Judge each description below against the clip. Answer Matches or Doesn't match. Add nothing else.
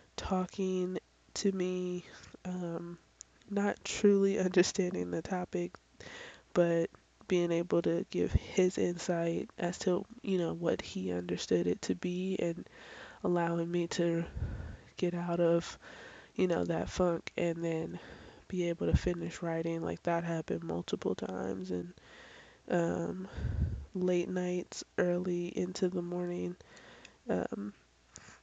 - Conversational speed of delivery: Doesn't match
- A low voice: Doesn't match